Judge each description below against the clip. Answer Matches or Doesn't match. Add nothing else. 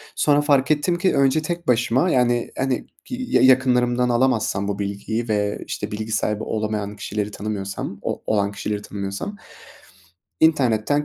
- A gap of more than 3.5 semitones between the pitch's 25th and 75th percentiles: Matches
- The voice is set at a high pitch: Doesn't match